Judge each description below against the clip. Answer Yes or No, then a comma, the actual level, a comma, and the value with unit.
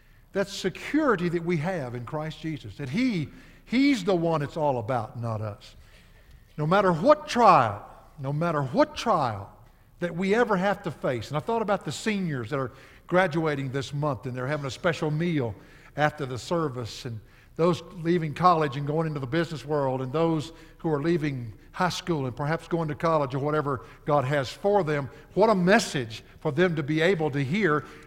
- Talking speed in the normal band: Yes, average, 190 wpm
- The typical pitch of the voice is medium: Yes, medium, 155 Hz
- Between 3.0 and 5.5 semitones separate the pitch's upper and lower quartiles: Yes, average, 4.6 semitones